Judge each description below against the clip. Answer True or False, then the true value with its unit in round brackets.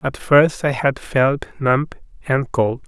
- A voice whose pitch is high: False (135 Hz)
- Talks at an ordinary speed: True (165 wpm)